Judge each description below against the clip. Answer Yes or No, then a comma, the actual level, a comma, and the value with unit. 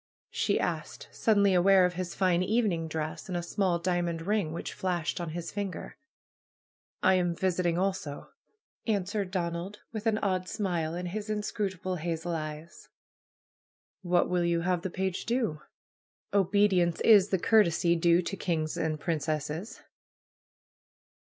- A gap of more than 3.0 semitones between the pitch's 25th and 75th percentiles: No, narrow, 2.6 semitones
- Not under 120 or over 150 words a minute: Yes, average, 140 wpm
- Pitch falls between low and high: Yes, medium, 180 Hz